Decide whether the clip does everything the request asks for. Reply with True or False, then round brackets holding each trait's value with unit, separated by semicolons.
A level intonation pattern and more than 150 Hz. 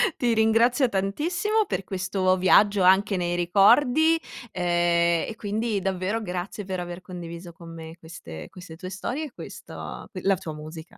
False (4.1 semitones; 185 Hz)